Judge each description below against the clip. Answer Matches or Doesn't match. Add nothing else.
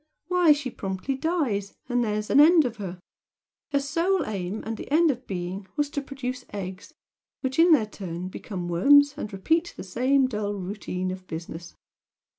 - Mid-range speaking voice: Doesn't match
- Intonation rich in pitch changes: Matches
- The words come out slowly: Doesn't match